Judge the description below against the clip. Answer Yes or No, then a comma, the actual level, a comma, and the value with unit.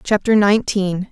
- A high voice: Yes, high, 200 Hz